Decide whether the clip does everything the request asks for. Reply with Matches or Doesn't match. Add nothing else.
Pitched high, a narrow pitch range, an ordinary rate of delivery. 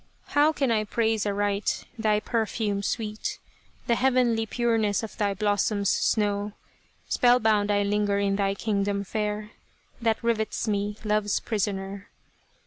Doesn't match